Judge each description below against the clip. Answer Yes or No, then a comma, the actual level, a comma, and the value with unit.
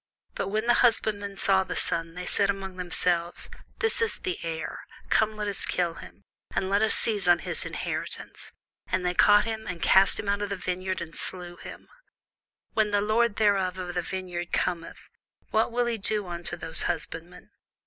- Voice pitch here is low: No, high, 190 Hz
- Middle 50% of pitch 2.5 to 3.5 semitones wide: Yes, average, 3.1 semitones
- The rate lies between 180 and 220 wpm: Yes, average, 190 wpm